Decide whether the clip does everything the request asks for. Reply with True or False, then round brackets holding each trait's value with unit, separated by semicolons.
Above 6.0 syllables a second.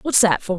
False (5.6 syllables/s)